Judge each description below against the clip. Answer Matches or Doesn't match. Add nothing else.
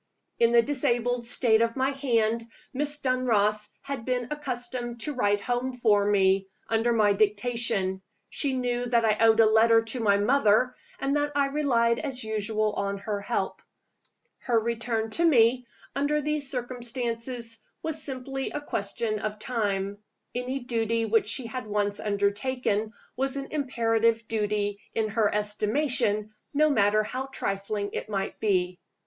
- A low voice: Doesn't match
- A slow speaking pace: Doesn't match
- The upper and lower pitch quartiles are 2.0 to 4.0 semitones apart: Matches